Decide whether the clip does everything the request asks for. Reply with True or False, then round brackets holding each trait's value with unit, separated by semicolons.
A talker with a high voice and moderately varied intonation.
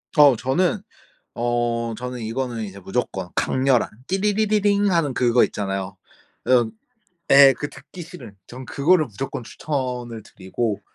False (125 Hz; 4.5 semitones)